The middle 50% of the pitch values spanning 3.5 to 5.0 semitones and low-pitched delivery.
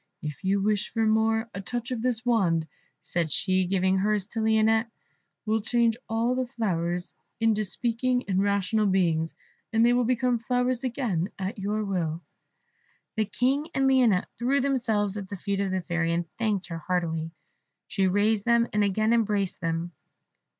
No: average, 3.9 semitones; high, 210 Hz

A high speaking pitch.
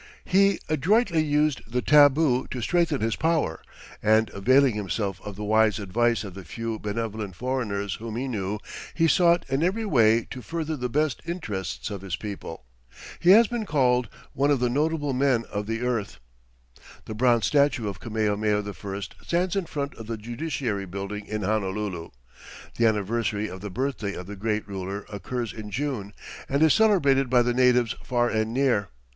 No: low, 115 Hz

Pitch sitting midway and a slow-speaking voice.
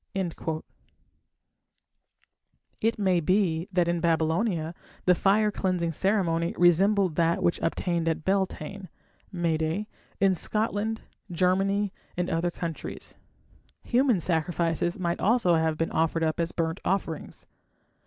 Yes: medium, 175 Hz; slow, 115 wpm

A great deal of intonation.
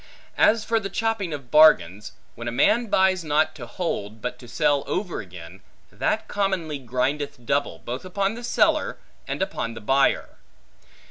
Yes: wide, 8.1 semitones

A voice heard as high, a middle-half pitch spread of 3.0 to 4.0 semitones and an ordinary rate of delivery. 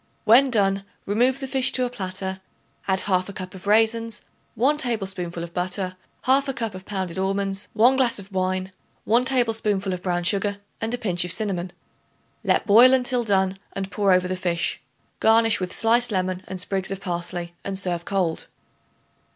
Yes: high, 195 Hz; average, 3.5 semitones; average, 175 wpm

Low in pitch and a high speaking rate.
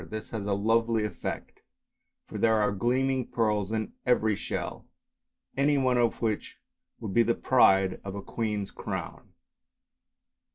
No: low, 110 Hz; average, 140 wpm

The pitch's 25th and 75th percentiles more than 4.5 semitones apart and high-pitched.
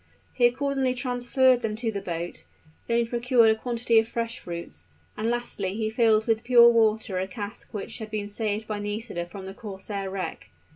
No: average, 2.7 semitones; high, 220 Hz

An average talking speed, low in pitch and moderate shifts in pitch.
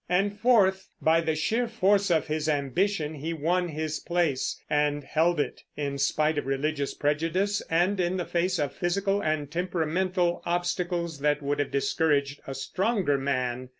No: average, 160 wpm; medium, 160 Hz; average, 3.8 semitones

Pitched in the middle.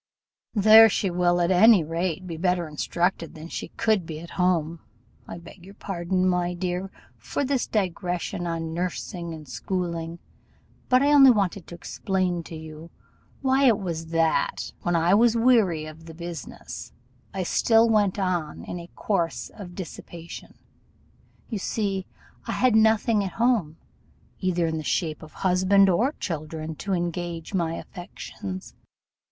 Yes: medium, 180 Hz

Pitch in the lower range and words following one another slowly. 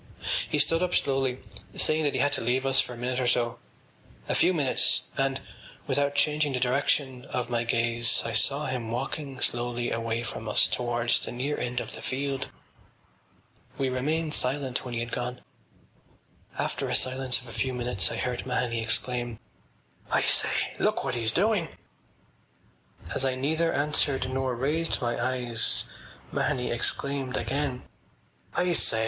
No: low, 130 Hz; average, 165 wpm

